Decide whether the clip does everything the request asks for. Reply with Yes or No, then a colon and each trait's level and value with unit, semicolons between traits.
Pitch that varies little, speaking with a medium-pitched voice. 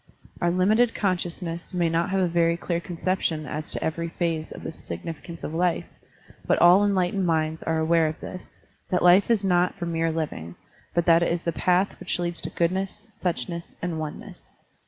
Yes: narrow, 1.8 semitones; medium, 170 Hz